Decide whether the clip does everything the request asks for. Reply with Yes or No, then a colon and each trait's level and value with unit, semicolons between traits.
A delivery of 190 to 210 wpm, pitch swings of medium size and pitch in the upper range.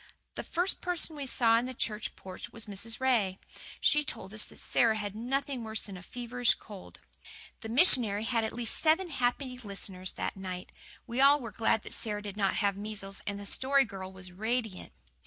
Yes: average, 195 wpm; average, 4.0 semitones; high, 225 Hz